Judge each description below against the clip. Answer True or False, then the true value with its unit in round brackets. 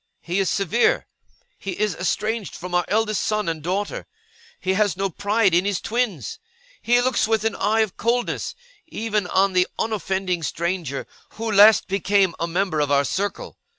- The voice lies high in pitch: True (195 Hz)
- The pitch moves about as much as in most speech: True (3.2 semitones)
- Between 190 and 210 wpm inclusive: False (170 wpm)